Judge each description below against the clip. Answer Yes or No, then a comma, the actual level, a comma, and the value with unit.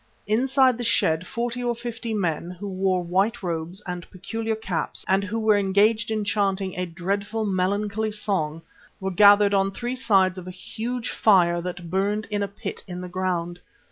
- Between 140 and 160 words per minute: No, average, 175 wpm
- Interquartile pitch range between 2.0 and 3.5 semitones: Yes, average, 3.2 semitones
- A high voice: Yes, high, 200 Hz